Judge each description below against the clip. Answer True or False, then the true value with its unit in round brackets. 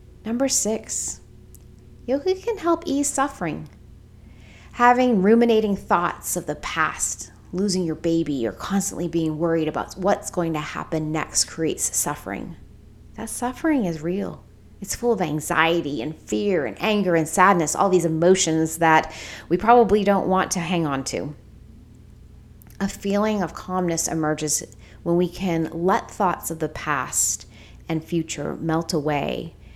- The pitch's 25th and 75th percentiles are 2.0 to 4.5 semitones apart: False (4.9 semitones)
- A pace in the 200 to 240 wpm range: False (145 wpm)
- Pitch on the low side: False (165 Hz)